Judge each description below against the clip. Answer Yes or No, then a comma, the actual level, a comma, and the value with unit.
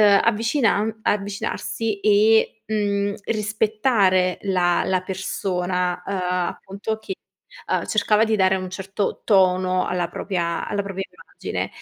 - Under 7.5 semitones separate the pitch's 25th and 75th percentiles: Yes, narrow, 2.6 semitones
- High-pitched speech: Yes, high, 200 Hz